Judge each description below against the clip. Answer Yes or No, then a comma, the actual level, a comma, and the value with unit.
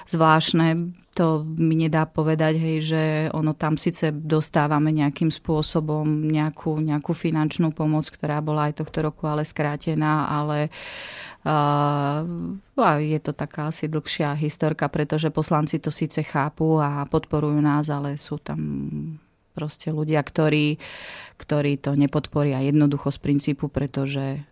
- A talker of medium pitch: Yes, medium, 155 Hz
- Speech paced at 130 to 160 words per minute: Yes, average, 135 wpm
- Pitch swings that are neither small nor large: No, narrow, 1.2 semitones